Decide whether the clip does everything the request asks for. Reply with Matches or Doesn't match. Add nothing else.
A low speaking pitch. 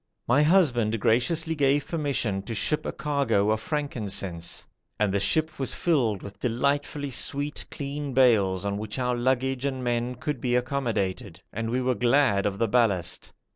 Matches